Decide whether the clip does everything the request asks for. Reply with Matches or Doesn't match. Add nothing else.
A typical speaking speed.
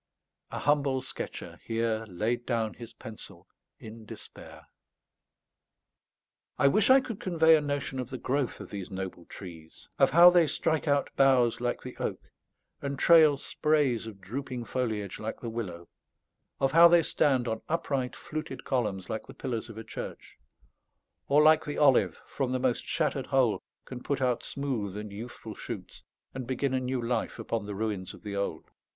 Matches